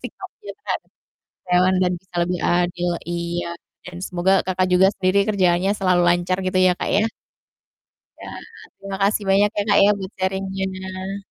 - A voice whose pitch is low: No, medium, 185 Hz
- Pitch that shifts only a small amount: Yes, narrow, 1.3 semitones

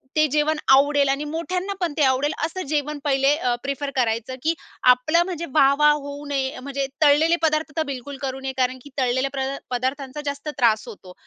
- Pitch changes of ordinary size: No, narrow, 2.3 semitones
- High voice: Yes, very high, 280 Hz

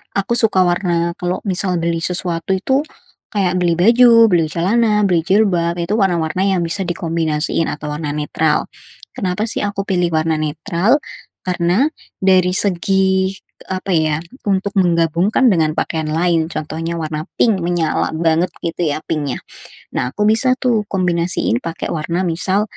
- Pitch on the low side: No, medium, 175 Hz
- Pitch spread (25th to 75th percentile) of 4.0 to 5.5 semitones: No, average, 3.0 semitones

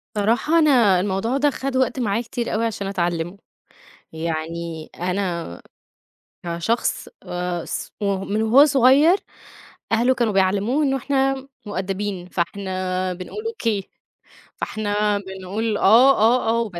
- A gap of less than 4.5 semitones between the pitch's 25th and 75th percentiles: No, average, 5.1 semitones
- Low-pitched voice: No, high, 205 Hz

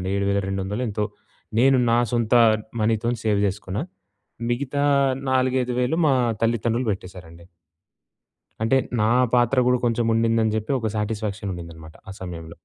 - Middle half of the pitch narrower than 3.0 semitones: No, average, 3.7 semitones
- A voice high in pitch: No, low, 110 Hz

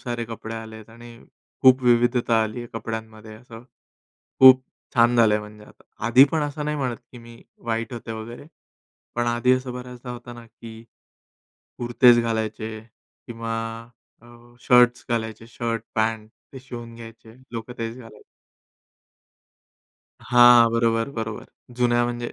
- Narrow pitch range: Yes, narrow, 1.4 semitones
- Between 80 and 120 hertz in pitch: Yes, low, 115 Hz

